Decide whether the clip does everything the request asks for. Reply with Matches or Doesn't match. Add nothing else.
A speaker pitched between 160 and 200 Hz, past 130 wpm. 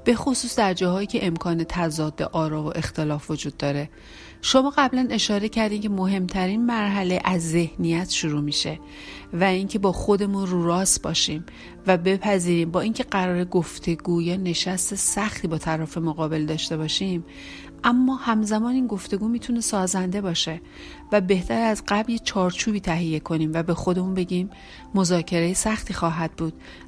Matches